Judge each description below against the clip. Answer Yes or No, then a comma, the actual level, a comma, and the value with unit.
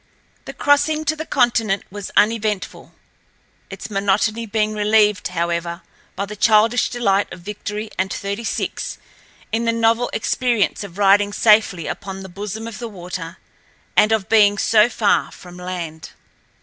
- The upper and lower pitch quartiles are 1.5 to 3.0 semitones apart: Yes, average, 2.7 semitones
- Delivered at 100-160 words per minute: Yes, average, 150 wpm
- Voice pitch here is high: Yes, high, 210 Hz